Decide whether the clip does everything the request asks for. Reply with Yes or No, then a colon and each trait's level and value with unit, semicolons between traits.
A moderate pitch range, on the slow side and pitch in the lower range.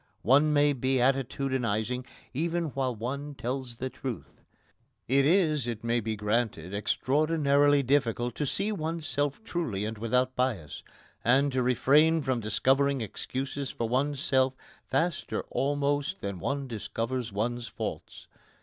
Yes: average, 3.4 semitones; slow, 130 wpm; low, 130 Hz